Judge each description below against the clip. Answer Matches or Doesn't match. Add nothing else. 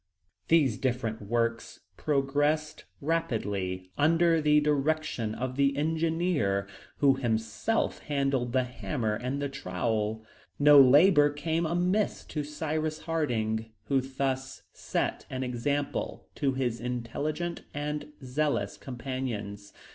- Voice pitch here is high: Doesn't match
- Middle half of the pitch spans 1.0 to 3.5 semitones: Doesn't match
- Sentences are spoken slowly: Matches